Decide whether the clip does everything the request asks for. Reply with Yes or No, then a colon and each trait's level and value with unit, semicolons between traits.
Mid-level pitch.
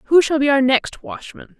No: very high, 275 Hz